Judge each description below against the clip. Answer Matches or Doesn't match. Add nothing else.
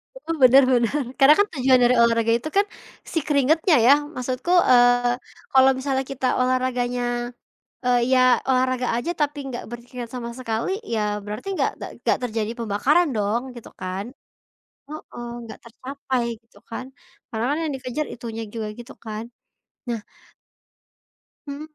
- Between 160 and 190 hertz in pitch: Doesn't match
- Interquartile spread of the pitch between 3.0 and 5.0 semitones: Doesn't match